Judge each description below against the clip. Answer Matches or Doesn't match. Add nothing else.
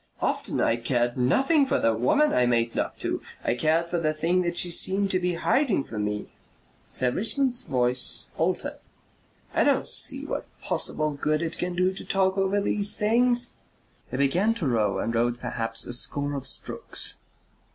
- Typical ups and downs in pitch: Doesn't match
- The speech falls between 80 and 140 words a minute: Doesn't match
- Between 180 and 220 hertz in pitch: Doesn't match